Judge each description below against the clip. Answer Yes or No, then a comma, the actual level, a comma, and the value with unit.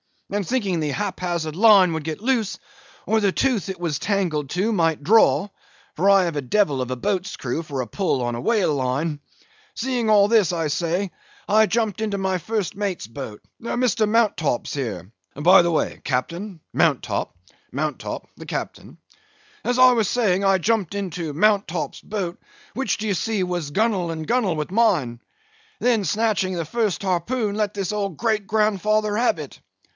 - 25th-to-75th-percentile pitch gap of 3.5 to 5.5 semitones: Yes, average, 5.1 semitones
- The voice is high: Yes, high, 195 Hz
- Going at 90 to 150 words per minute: No, average, 170 wpm